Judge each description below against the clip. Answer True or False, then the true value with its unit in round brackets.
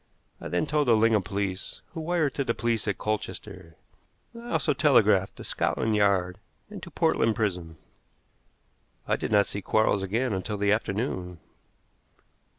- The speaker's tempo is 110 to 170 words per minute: True (155 wpm)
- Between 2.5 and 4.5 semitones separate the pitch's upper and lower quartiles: True (3.4 semitones)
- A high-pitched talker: False (105 Hz)